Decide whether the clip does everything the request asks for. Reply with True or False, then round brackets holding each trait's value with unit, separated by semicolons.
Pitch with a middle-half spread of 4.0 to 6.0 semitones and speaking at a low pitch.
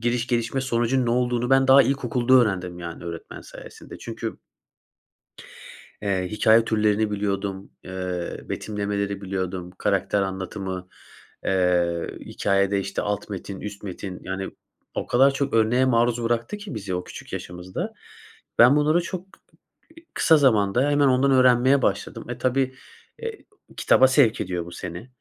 True (5.2 semitones; 110 Hz)